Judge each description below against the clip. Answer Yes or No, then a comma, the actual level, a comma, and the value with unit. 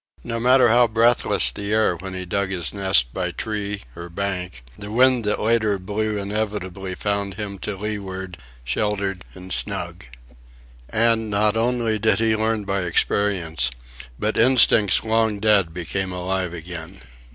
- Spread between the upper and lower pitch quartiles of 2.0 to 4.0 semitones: Yes, average, 2.9 semitones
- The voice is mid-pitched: No, low, 100 Hz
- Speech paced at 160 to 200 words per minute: No, average, 150 wpm